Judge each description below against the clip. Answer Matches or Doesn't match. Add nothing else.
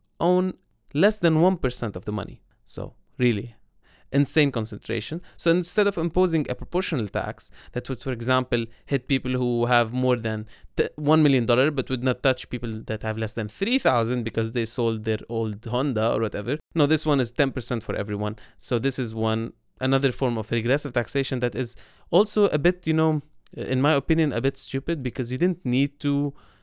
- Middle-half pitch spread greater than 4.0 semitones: Matches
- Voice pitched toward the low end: Matches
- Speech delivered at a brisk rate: Doesn't match